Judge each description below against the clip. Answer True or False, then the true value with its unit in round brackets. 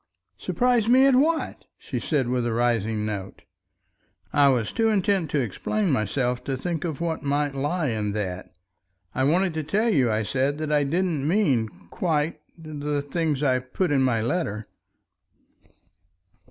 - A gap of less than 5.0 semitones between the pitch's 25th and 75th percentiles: False (5.6 semitones)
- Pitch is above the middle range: False (145 Hz)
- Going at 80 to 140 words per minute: False (160 wpm)